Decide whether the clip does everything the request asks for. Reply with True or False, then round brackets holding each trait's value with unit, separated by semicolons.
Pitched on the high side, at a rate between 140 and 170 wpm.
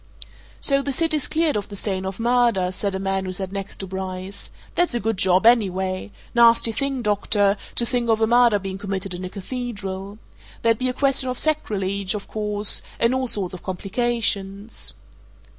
False (205 Hz; 185 wpm)